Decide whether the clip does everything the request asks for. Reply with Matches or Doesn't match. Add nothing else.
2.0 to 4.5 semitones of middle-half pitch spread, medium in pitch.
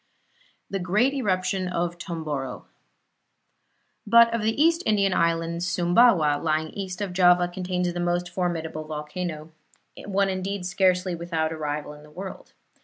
Matches